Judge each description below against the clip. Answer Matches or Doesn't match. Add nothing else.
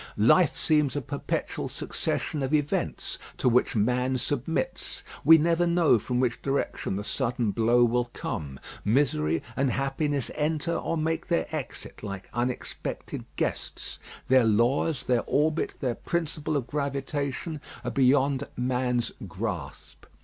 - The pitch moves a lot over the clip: Doesn't match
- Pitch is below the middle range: Matches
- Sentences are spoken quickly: Doesn't match